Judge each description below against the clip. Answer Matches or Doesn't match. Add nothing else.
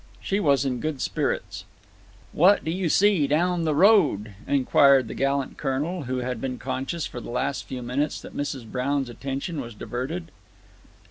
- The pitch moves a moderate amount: Matches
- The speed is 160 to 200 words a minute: Matches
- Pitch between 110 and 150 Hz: Matches